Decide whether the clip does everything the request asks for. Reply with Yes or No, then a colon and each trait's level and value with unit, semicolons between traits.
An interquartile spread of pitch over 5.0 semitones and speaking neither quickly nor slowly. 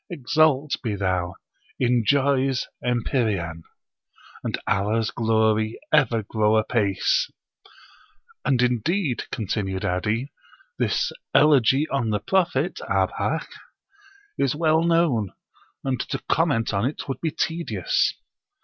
No: wide, 5.5 semitones; slow, 105 wpm